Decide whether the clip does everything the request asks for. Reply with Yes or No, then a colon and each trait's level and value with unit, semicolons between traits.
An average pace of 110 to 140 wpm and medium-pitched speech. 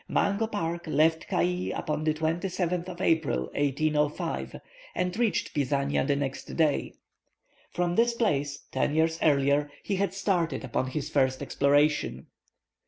Yes: slow, 135 wpm; medium, 160 Hz